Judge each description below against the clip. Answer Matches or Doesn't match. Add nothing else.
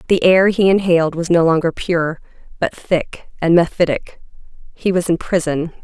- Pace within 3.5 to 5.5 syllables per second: Matches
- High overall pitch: Doesn't match